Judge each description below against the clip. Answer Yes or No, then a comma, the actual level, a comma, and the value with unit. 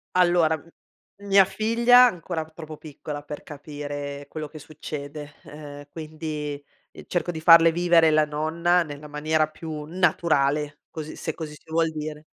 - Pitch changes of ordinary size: No, narrow, 2.0 semitones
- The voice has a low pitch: No, medium, 155 Hz